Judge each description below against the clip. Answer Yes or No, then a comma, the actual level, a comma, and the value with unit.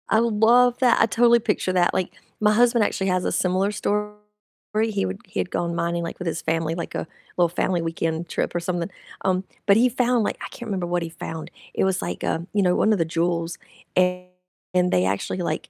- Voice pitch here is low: No, medium, 180 Hz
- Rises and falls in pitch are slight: No, average, 4.0 semitones